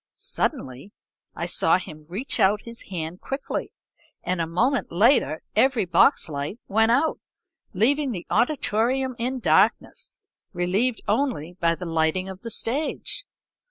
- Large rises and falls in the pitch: Yes, wide, 6.5 semitones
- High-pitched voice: Yes, high, 205 Hz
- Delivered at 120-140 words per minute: Yes, slow, 135 wpm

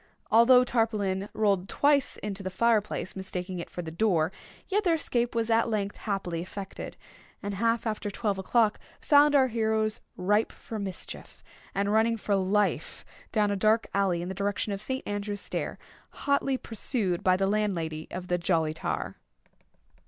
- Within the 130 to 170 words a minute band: Yes, average, 165 wpm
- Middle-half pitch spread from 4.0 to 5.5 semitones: No, average, 3.2 semitones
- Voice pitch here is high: Yes, high, 205 Hz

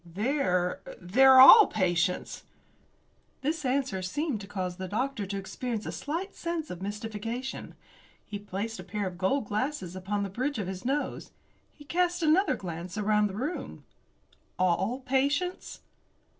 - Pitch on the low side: No, high, 215 Hz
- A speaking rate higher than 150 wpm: No, average, 145 wpm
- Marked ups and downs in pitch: Yes, wide, 6.6 semitones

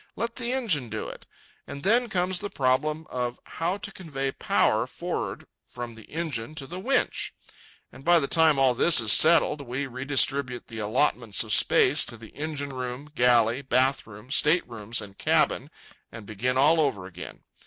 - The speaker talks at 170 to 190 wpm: Yes, average, 175 wpm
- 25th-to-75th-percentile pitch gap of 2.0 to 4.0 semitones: No, average, 5.0 semitones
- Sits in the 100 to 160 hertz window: Yes, low, 135 Hz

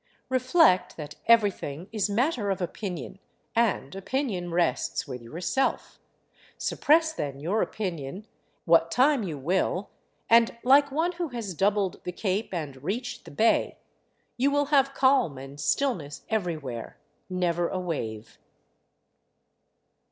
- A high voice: Yes, high, 195 Hz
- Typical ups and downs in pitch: No, wide, 7.2 semitones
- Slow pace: Yes, slow, 125 wpm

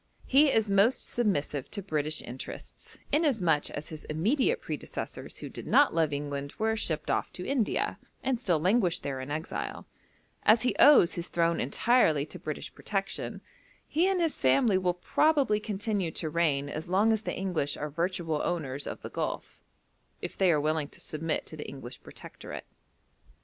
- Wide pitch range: Yes, wide, 6.6 semitones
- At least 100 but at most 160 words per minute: No, average, 170 wpm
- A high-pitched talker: No, medium, 175 Hz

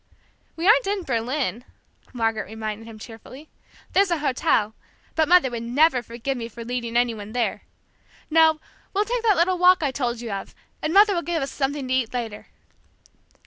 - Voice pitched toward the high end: Yes, very high, 260 Hz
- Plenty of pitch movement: Yes, wide, 6.2 semitones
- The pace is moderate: Yes, average, 185 wpm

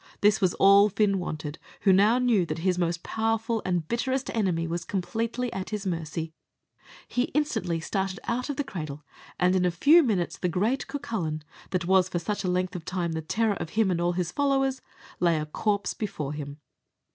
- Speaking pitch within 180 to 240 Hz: Yes, medium, 185 Hz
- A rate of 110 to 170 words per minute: No, average, 195 wpm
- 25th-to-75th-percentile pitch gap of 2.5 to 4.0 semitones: No, average, 4.6 semitones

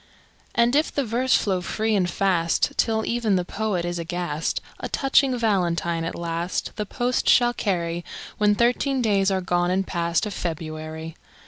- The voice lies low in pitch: No, high, 190 Hz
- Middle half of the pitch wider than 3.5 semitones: Yes, average, 4.7 semitones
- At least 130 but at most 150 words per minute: No, average, 165 wpm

